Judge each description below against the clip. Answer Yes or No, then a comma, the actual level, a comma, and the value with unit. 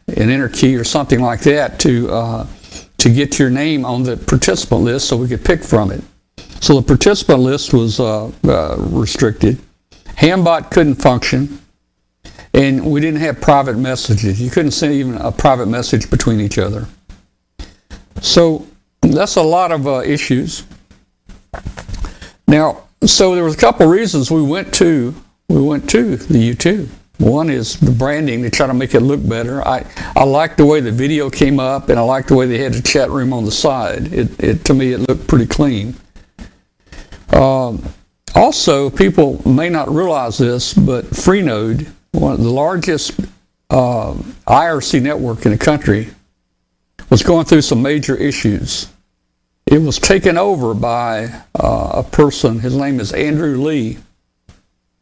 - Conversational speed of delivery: Yes, average, 165 wpm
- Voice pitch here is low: Yes, low, 130 Hz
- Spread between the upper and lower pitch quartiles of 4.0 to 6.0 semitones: Yes, average, 4.5 semitones